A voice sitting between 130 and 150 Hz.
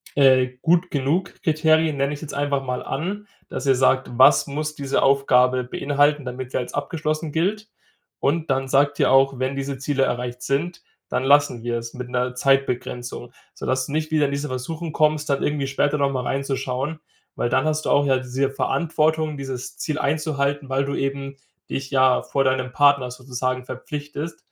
Yes: medium, 140 Hz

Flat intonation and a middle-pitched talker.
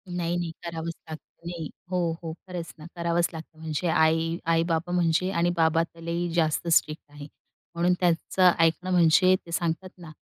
Yes: narrow, 1.3 semitones; medium, 170 Hz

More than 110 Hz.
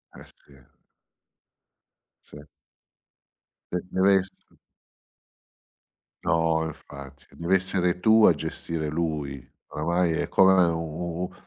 No: very low, 85 Hz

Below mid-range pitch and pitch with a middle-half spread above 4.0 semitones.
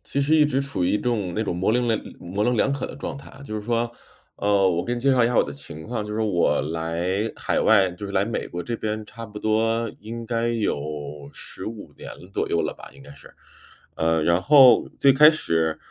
Yes: low, 110 Hz; average, 5.2 semitones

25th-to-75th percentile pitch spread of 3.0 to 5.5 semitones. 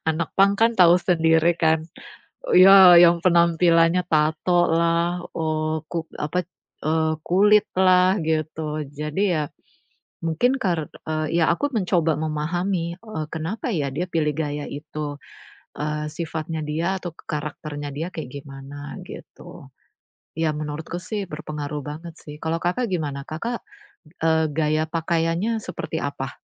No: narrow, 2.6 semitones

